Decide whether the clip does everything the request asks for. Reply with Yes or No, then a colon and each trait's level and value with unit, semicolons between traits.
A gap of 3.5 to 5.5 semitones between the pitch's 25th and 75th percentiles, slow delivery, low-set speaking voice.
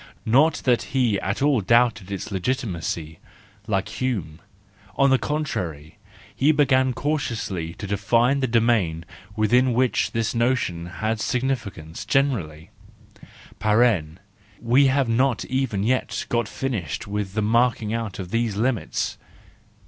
Yes: average, 5.0 semitones; slow, 125 wpm; low, 115 Hz